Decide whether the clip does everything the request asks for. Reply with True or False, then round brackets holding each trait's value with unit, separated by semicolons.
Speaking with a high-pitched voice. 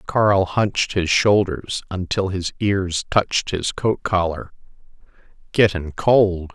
False (95 Hz)